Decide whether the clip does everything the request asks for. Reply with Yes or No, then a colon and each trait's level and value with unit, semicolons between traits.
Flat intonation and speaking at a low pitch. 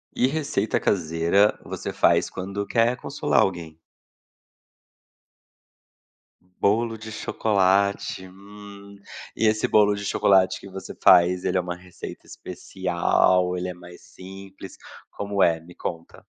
Yes: narrow, 2.2 semitones; very low, 95 Hz